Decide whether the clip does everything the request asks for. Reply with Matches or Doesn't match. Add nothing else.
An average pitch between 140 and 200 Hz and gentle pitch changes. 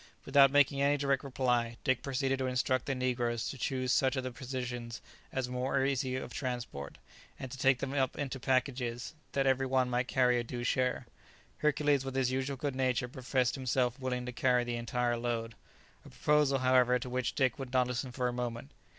Doesn't match